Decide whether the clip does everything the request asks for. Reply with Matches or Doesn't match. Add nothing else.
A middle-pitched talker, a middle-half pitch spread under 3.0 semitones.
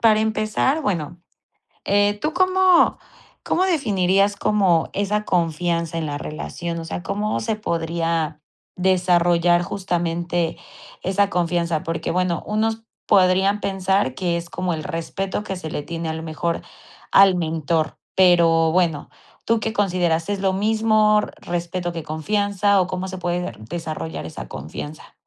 Doesn't match